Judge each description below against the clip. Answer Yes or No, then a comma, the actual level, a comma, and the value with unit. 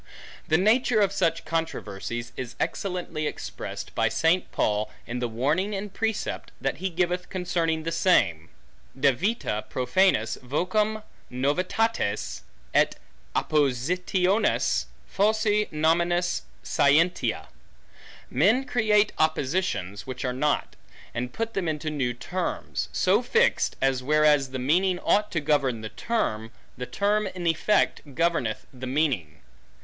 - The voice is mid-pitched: Yes, medium, 160 Hz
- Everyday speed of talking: No, slow, 125 wpm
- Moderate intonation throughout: No, wide, 6.7 semitones